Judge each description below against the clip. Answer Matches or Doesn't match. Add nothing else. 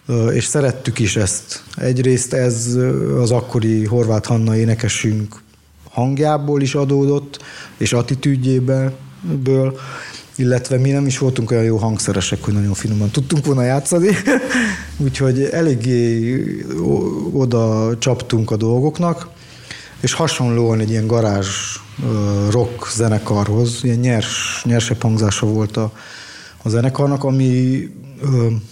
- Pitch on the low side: Matches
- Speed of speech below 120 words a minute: Matches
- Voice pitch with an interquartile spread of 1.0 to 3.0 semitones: Doesn't match